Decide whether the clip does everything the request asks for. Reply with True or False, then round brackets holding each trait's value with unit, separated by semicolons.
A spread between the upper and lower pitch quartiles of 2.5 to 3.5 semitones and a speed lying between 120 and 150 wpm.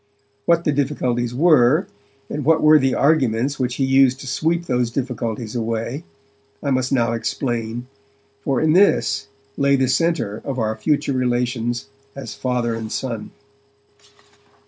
True (3.2 semitones; 145 wpm)